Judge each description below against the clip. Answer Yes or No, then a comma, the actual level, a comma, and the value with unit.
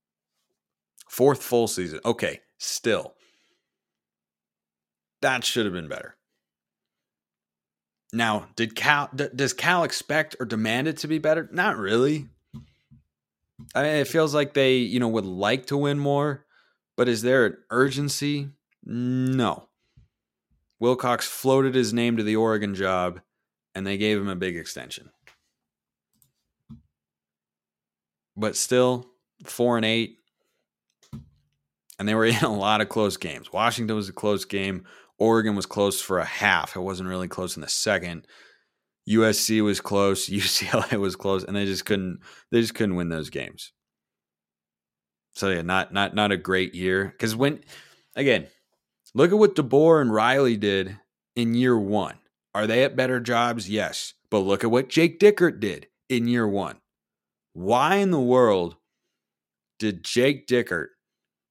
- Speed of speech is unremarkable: Yes, average, 145 wpm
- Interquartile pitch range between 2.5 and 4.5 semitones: No, wide, 5.5 semitones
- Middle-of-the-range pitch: No, low, 110 Hz